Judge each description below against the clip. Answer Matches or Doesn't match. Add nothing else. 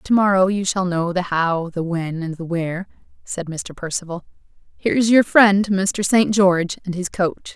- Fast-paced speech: Doesn't match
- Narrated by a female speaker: Matches